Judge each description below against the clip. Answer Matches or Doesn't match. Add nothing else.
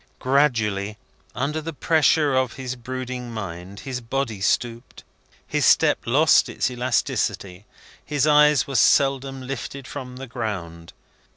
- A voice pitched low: Matches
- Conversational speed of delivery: Doesn't match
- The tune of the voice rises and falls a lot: Doesn't match